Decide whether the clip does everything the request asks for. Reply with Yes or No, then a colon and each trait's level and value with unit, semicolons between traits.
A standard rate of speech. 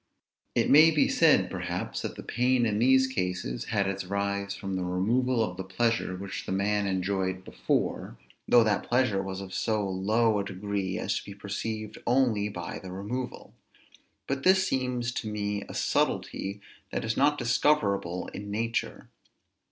Yes: average, 165 wpm